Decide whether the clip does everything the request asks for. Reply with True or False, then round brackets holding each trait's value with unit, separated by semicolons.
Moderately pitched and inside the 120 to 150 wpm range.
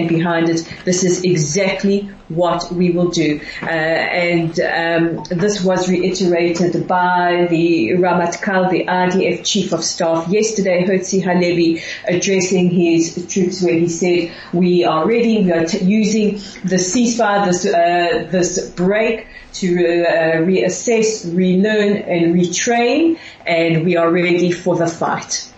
True (180 Hz; 140 wpm)